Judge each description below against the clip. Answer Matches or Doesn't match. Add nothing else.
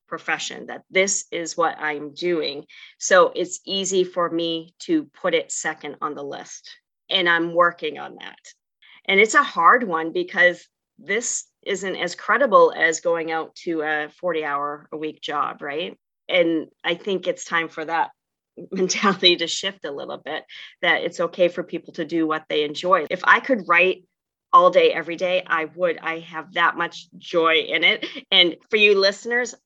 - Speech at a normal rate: Matches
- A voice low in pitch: Doesn't match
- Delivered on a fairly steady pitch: Doesn't match